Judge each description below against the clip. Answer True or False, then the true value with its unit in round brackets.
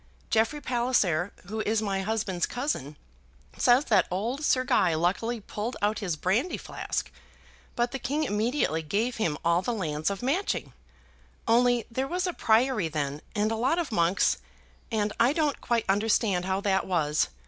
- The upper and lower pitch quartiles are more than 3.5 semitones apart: True (5.0 semitones)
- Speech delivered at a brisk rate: False (165 wpm)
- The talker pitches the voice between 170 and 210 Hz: False (220 Hz)